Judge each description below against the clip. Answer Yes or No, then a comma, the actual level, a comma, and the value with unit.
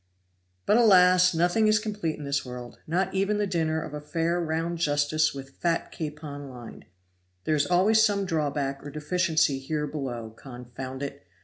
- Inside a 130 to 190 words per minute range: Yes, average, 170 wpm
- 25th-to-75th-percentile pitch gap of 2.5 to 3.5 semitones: No, average, 4.3 semitones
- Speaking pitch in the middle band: Yes, medium, 155 Hz